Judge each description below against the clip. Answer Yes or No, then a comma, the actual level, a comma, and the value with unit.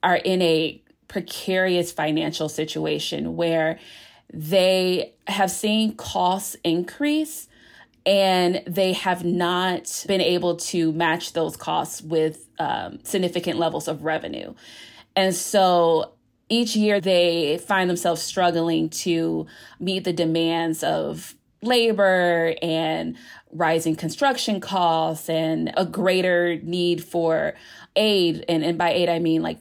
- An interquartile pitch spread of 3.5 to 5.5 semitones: No, average, 2.7 semitones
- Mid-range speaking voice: Yes, medium, 175 Hz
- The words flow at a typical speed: No, slow, 120 wpm